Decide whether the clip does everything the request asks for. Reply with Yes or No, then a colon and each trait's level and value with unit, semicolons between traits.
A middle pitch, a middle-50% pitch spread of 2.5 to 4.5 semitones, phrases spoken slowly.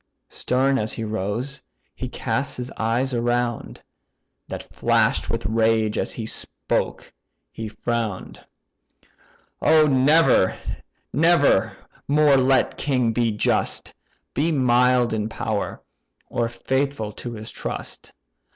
No: low, 120 Hz; average, 3.4 semitones; slow, 115 wpm